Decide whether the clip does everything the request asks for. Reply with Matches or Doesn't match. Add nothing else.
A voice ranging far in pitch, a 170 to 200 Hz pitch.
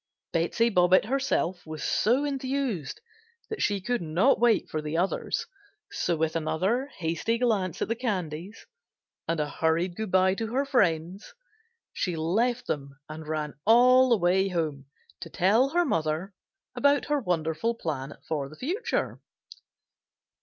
Matches